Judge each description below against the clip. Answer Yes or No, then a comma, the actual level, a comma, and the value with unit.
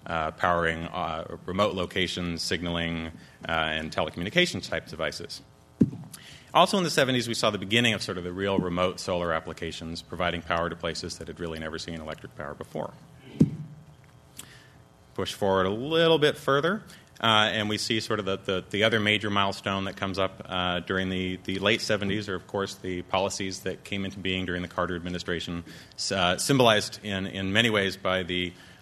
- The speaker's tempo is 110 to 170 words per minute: No, average, 180 wpm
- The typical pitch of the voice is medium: No, very low, 95 Hz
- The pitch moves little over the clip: No, average, 3.4 semitones